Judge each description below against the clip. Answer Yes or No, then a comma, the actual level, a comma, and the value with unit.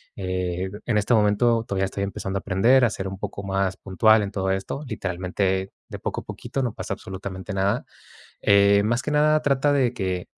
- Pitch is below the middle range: Yes, low, 100 Hz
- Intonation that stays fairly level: No, average, 3.5 semitones